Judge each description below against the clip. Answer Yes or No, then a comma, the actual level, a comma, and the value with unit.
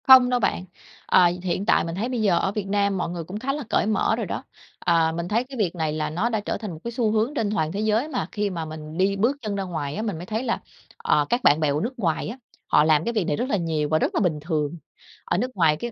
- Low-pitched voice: No, high, 195 Hz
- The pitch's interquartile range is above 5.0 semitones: Yes, wide, 5.6 semitones